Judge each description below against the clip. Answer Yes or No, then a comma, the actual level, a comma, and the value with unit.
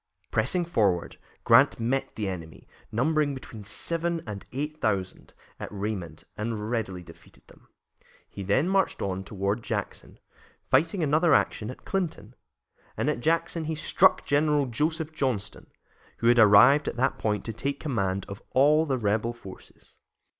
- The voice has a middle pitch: No, low, 120 Hz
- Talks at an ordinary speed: Yes, average, 150 wpm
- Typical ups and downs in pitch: No, wide, 6.9 semitones